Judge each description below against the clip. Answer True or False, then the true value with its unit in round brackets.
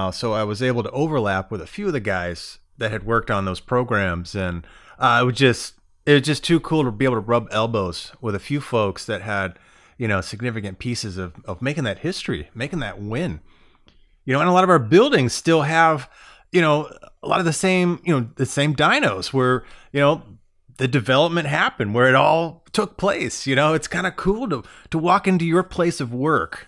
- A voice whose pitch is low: True (130 Hz)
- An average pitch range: False (6.9 semitones)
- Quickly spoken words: True (220 wpm)